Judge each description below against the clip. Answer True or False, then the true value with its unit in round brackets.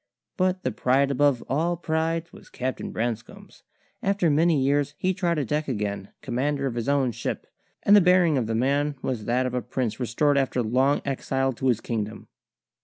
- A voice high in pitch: False (135 Hz)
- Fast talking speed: False (185 wpm)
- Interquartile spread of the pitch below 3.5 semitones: False (4.0 semitones)